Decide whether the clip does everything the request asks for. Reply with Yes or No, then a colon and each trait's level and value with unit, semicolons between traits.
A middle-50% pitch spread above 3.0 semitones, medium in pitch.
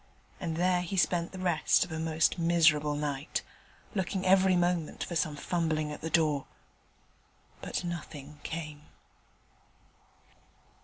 No: average, 2.7 semitones; medium, 165 Hz